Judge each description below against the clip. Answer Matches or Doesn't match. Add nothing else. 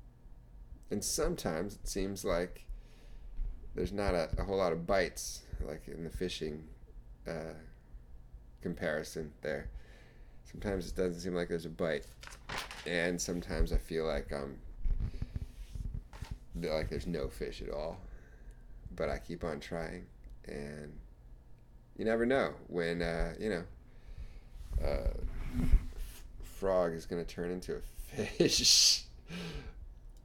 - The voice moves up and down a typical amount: Doesn't match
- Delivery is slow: Matches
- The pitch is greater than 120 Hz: Doesn't match